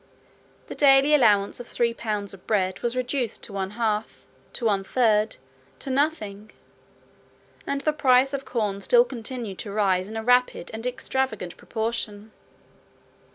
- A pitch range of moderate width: Yes, average, 3.9 semitones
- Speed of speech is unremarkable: Yes, average, 150 wpm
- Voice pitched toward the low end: No, high, 225 Hz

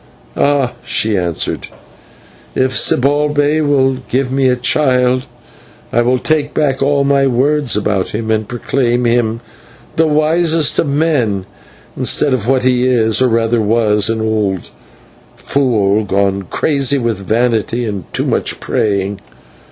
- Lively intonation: No, average, 4.2 semitones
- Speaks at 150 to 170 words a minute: No, slow, 135 wpm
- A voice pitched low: Yes, low, 125 Hz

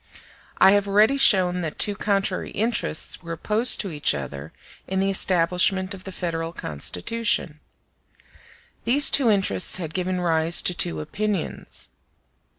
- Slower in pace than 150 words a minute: Yes, average, 140 wpm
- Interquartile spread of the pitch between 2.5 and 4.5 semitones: Yes, average, 3.7 semitones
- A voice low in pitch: No, medium, 185 Hz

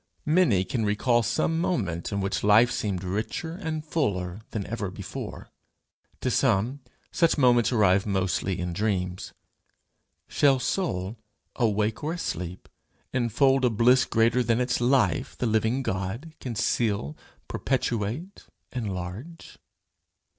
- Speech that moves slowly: Yes, slow, 125 wpm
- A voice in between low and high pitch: No, low, 115 Hz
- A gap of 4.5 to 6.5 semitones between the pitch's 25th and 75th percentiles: Yes, average, 5.1 semitones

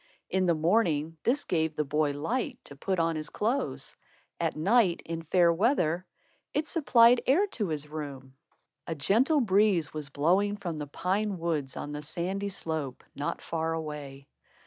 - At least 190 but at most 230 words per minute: No, average, 165 wpm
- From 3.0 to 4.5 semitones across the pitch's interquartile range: No, average, 5.2 semitones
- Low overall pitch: No, medium, 165 Hz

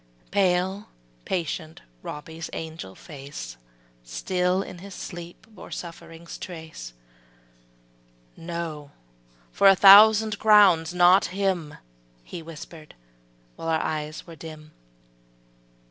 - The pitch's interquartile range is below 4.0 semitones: Yes, average, 3.0 semitones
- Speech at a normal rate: No, slow, 100 wpm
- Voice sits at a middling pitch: Yes, medium, 170 Hz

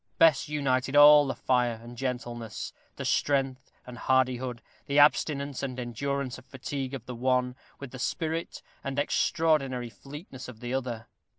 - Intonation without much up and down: Yes, narrow, 2.2 semitones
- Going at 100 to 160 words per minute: Yes, average, 155 wpm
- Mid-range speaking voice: No, low, 130 Hz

